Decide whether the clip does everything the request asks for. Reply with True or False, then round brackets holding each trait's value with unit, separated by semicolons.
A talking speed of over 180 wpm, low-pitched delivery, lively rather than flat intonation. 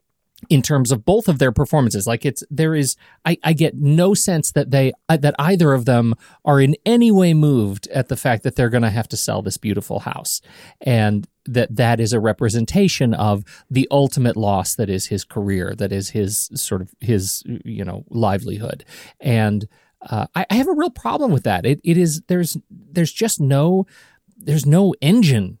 True (190 wpm; 130 Hz; 6.6 semitones)